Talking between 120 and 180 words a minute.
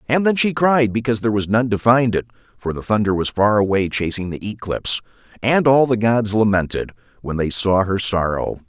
No: fast, 205 wpm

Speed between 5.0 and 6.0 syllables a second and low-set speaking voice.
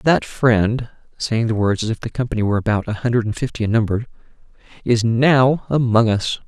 Yes: 5.4 syllables/s; low, 115 Hz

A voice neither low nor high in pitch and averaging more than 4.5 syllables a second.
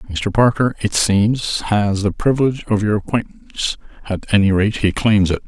No: low, 105 Hz; 5.1 syllables/s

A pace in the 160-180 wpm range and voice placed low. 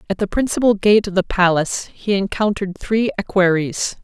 No: average, 165 wpm; high, 195 Hz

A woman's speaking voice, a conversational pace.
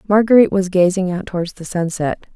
Yes: female; average, 180 wpm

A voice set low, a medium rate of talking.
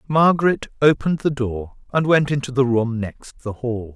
Yes: low, 130 Hz; average, 180 wpm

